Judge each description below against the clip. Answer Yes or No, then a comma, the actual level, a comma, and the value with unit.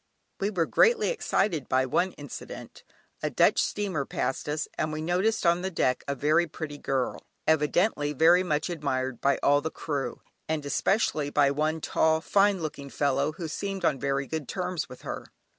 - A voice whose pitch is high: No, medium, 155 Hz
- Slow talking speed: No, average, 175 wpm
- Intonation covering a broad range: No, average, 3.9 semitones